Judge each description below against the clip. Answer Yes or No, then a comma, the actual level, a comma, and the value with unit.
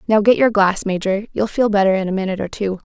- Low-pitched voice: No, high, 200 Hz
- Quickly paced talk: Yes, fast, 270 wpm